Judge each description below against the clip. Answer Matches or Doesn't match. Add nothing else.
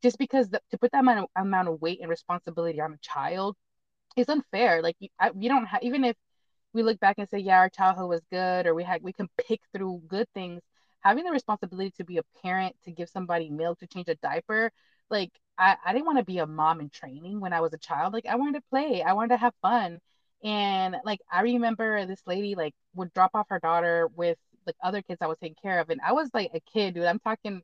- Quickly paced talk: Matches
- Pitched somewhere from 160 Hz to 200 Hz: Matches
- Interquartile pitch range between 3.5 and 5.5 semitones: Matches